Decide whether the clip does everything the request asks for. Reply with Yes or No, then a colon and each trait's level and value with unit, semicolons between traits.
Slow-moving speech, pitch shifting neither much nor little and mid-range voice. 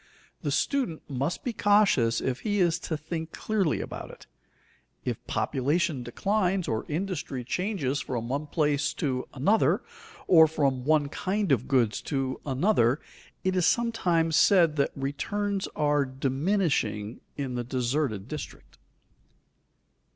No: slow, 130 wpm; wide, 5.9 semitones; medium, 150 Hz